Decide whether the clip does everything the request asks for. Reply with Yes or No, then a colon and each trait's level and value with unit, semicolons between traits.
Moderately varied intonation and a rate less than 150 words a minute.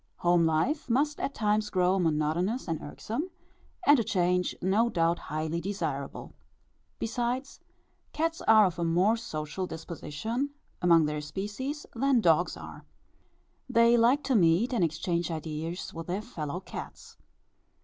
No: wide, 6.1 semitones; average, 140 wpm